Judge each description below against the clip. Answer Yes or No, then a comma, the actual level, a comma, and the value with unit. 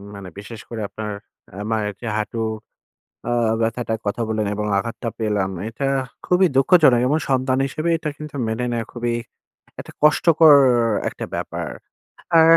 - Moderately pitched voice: No, low, 120 Hz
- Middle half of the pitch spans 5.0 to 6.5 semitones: Yes, average, 5.3 semitones